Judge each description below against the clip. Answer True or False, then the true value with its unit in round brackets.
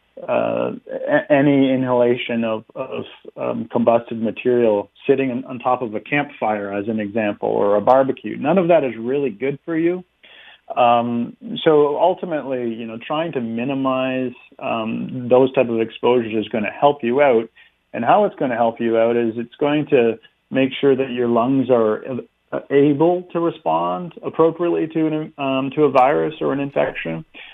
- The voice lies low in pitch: True (125 Hz)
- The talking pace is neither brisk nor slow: True (170 wpm)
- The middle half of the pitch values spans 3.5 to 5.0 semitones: True (3.9 semitones)